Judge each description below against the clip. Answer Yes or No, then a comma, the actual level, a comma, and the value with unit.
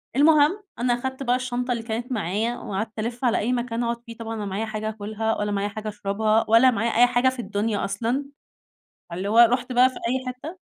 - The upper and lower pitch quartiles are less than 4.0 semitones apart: Yes, narrow, 2.5 semitones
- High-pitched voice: Yes, high, 230 Hz